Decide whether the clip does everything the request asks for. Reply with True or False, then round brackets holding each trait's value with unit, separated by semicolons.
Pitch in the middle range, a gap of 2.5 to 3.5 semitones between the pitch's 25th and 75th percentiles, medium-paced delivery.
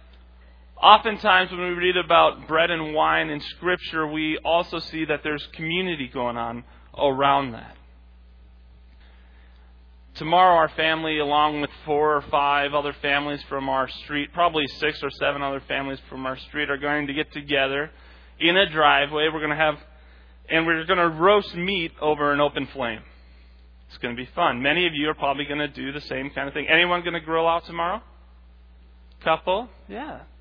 False (145 Hz; 5.6 semitones; 180 wpm)